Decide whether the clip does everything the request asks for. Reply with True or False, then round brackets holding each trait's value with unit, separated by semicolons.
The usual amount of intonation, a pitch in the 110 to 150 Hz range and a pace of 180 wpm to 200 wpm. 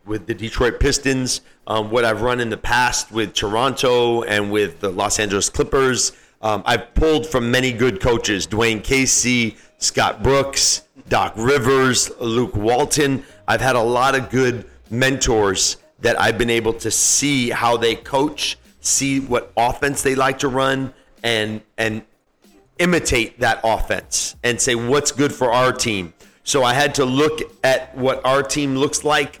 False (3.1 semitones; 125 Hz; 165 wpm)